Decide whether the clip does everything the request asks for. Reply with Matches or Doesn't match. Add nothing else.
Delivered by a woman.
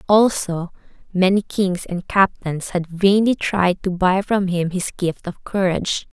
Matches